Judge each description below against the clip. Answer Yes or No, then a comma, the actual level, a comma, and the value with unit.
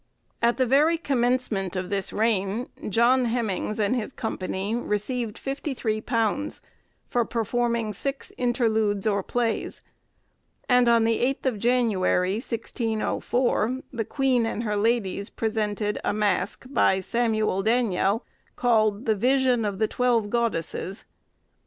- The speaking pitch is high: Yes, high, 225 Hz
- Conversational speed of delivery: No, slow, 125 wpm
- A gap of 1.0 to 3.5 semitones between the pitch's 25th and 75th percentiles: Yes, average, 2.9 semitones